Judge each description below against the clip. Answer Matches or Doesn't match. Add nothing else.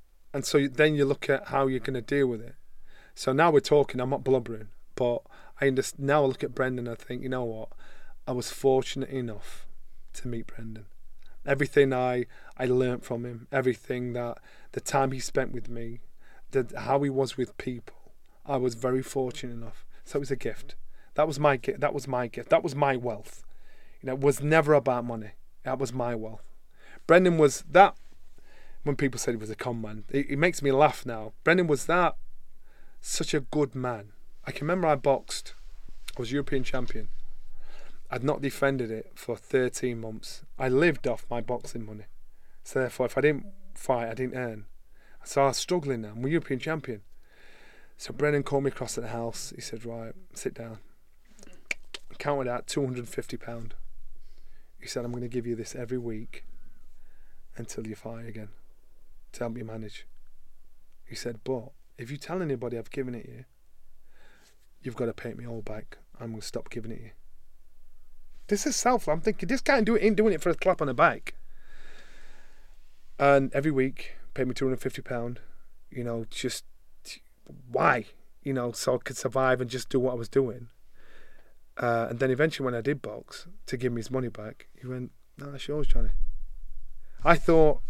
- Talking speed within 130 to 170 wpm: Doesn't match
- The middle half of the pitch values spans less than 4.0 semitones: Matches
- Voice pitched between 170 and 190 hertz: Doesn't match